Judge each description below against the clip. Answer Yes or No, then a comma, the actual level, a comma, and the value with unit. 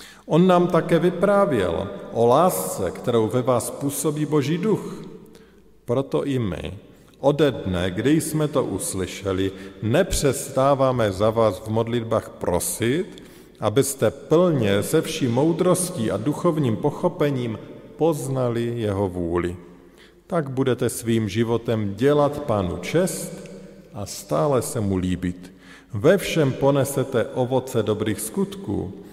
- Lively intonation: Yes, wide, 7.3 semitones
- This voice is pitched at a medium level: No, low, 125 Hz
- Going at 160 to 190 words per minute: No, average, 115 wpm